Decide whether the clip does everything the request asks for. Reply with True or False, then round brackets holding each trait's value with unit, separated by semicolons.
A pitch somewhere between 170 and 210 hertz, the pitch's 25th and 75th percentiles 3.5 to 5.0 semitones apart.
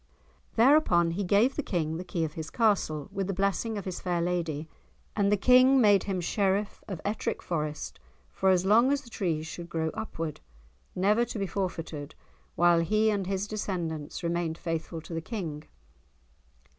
True (185 Hz; 4.0 semitones)